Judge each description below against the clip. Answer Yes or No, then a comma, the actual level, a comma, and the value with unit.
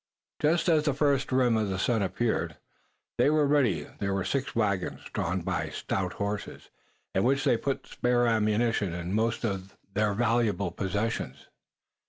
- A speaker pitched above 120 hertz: No, low, 115 Hz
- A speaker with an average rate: Yes, average, 160 wpm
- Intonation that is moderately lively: Yes, average, 4.7 semitones